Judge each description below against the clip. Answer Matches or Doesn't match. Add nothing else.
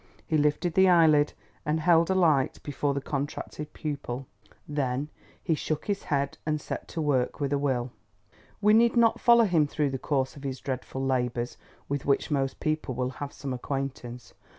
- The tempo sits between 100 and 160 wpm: Doesn't match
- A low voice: Doesn't match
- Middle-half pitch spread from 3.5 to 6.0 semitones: Doesn't match